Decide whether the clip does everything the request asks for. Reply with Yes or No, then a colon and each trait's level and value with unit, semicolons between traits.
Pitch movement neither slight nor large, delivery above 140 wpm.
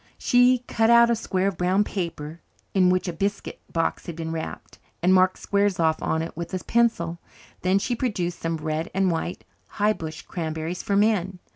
Yes: average, 3.6 semitones; average, 190 wpm